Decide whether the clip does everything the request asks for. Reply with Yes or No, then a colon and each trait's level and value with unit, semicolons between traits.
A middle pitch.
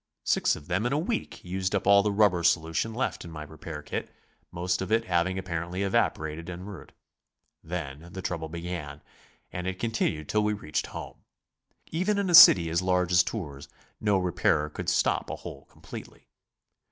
No: very low, 90 Hz